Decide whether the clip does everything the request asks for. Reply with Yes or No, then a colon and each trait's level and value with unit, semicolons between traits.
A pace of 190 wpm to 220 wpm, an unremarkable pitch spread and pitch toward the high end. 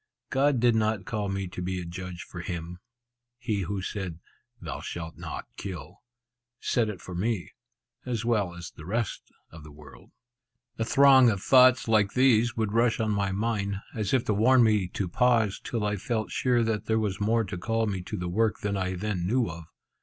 No: average, 200 wpm; average, 3.8 semitones; low, 105 Hz